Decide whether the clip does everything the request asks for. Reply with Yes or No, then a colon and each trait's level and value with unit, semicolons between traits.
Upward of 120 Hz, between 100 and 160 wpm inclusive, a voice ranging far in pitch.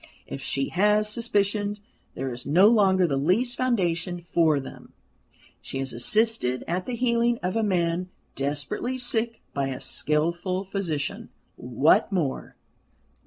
Yes: medium, 185 Hz; slow, 135 wpm; wide, 6.5 semitones